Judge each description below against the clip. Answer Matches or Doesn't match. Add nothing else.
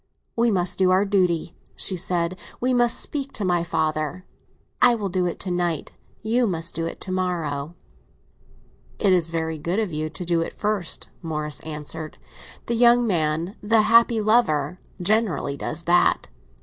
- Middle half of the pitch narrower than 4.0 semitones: Doesn't match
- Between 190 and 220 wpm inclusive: Doesn't match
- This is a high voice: Doesn't match